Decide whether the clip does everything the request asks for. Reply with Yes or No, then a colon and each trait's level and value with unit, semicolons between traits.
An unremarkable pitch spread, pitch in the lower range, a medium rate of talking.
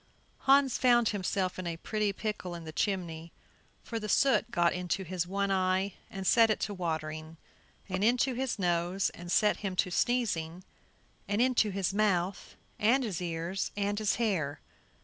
No: average, 3.6 semitones; high, 195 Hz; average, 170 wpm